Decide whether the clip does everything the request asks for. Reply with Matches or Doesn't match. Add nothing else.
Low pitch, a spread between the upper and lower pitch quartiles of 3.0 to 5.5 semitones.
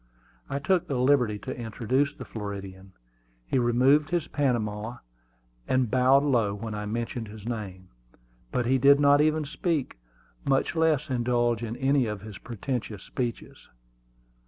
Matches